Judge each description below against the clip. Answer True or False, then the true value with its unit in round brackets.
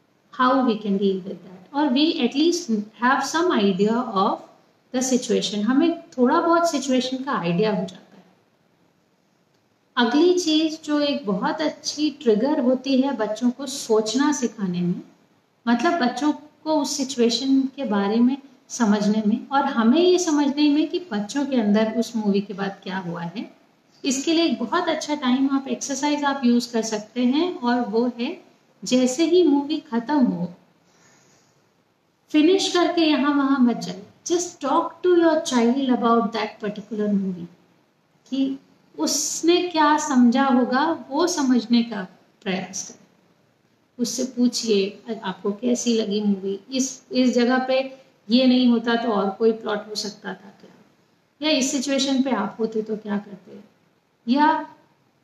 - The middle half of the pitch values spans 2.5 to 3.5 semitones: False (5.5 semitones)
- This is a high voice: True (250 Hz)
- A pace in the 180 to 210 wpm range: False (150 wpm)